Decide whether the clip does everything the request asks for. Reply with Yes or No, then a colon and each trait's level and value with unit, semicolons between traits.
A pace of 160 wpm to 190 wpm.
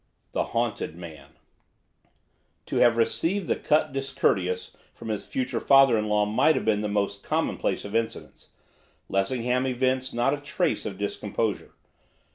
No: average, 145 wpm